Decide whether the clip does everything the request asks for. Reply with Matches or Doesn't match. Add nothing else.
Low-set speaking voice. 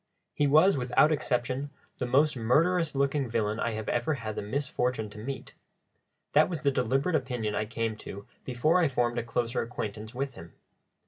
Matches